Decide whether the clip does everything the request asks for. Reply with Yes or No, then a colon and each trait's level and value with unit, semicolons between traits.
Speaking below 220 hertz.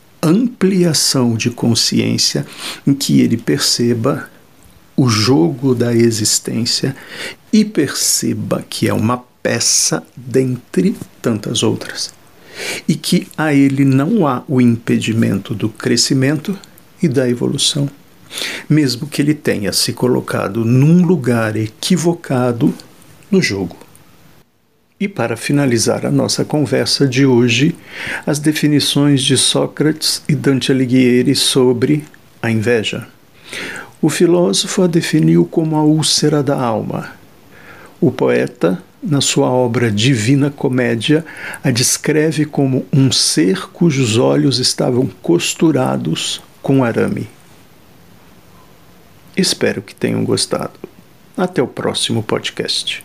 Yes: medium, 140 Hz